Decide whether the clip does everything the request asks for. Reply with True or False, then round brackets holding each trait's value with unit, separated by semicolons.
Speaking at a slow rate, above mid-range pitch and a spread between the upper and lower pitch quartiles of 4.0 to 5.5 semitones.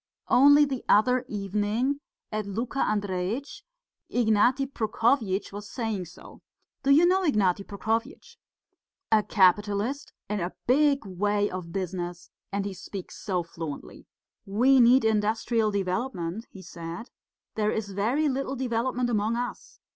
True (130 wpm; 215 Hz; 4.3 semitones)